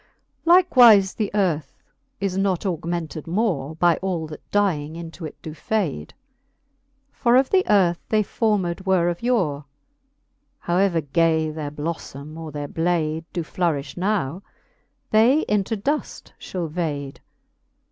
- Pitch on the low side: No, medium, 175 Hz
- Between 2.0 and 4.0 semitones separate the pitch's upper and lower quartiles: No, average, 4.5 semitones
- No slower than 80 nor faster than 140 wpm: Yes, slow, 135 wpm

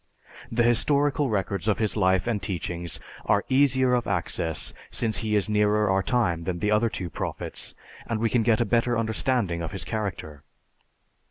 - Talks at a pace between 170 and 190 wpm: Yes, average, 175 wpm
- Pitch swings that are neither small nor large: Yes, average, 3.9 semitones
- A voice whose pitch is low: Yes, low, 105 Hz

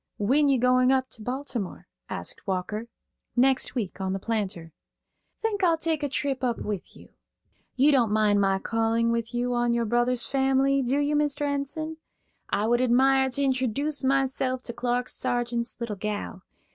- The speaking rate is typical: Yes, average, 170 wpm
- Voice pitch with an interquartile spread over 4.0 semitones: No, average, 3.2 semitones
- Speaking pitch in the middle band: No, very high, 250 Hz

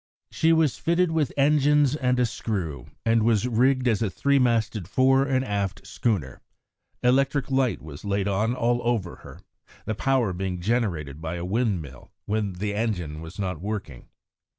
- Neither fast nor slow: Yes, average, 165 wpm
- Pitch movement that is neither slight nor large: No, wide, 5.7 semitones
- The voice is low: Yes, low, 110 Hz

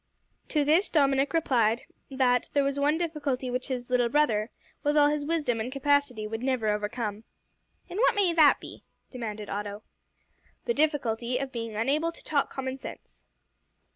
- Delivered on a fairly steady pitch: No, average, 4.3 semitones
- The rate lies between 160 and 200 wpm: Yes, average, 165 wpm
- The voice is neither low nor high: No, very high, 265 Hz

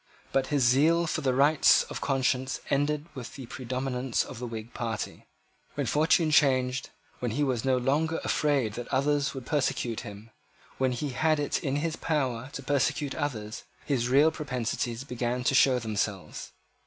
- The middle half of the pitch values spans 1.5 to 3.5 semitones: Yes, average, 3.0 semitones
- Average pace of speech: Yes, average, 165 wpm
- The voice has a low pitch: Yes, low, 130 Hz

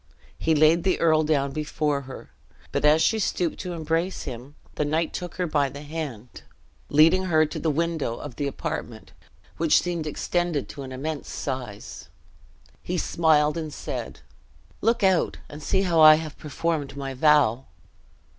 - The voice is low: No, medium, 155 Hz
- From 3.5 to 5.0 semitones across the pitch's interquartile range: No, average, 2.7 semitones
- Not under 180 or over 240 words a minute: No, average, 165 wpm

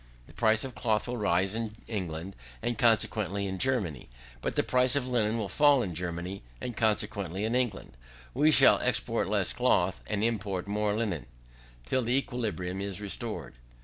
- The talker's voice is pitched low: Yes, low, 105 Hz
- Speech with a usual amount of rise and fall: Yes, average, 4.0 semitones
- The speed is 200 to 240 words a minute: No, average, 170 wpm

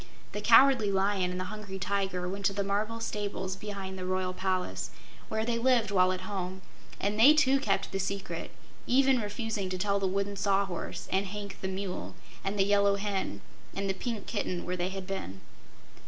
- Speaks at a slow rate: No, average, 190 wpm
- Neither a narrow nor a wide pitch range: No, narrow, 1.8 semitones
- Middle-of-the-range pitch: No, high, 200 Hz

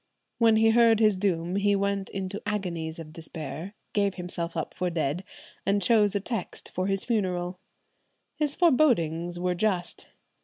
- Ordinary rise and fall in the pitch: Yes, average, 3.3 semitones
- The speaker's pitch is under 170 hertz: No, high, 195 Hz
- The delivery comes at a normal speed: Yes, average, 155 wpm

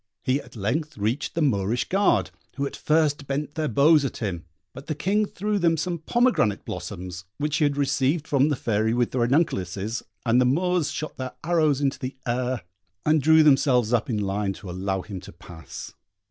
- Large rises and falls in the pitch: Yes, wide, 6.0 semitones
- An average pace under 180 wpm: No, average, 195 wpm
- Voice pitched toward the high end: No, low, 135 Hz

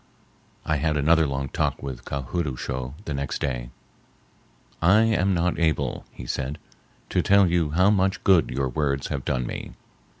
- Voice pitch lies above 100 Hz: No, very low, 75 Hz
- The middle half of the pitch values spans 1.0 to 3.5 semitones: No, average, 4.7 semitones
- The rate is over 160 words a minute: Yes, average, 175 wpm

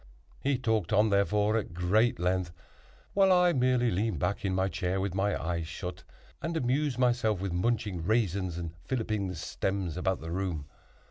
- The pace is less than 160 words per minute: No, average, 175 wpm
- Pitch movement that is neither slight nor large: Yes, average, 4.9 semitones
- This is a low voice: Yes, low, 100 Hz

